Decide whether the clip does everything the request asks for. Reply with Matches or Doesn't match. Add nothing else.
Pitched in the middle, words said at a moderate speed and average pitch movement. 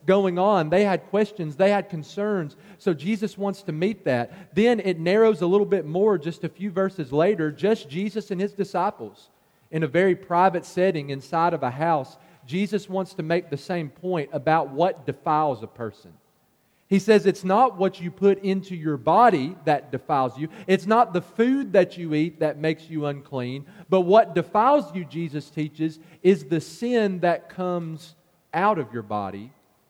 Matches